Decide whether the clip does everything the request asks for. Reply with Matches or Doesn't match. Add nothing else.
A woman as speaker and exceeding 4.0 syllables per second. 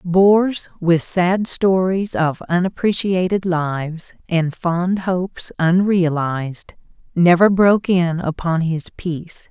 Doesn't match